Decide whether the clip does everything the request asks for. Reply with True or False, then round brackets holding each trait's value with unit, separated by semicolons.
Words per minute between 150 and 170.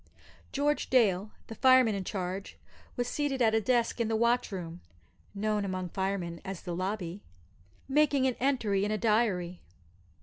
True (160 wpm)